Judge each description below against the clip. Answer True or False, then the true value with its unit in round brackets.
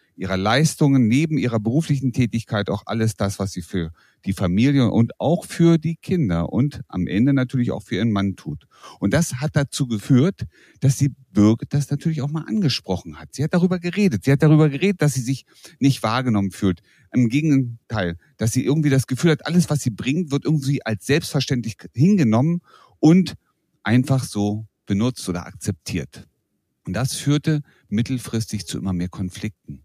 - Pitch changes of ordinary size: False (6.0 semitones)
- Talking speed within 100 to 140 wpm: False (175 wpm)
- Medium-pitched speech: False (130 Hz)